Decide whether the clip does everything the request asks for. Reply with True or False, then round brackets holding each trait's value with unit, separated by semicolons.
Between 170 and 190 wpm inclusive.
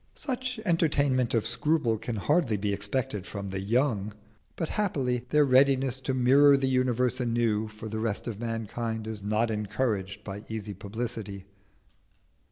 False (150 wpm)